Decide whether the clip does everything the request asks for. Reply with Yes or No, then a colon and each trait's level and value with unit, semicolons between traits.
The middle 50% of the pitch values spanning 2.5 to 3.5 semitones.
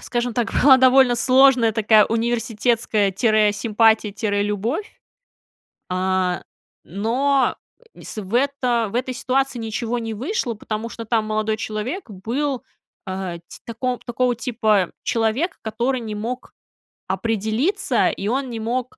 Yes: average, 2.9 semitones